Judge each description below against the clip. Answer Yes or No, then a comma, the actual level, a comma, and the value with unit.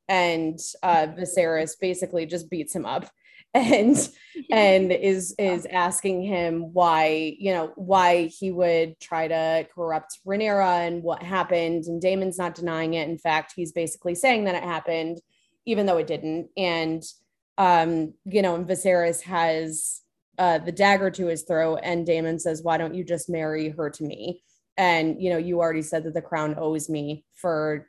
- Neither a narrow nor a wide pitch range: No, narrow, 2.2 semitones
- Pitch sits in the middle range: Yes, medium, 170 Hz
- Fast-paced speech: No, average, 170 wpm